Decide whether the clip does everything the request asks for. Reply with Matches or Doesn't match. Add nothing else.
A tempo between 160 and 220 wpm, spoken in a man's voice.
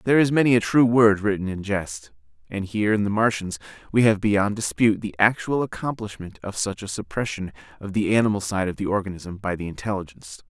Matches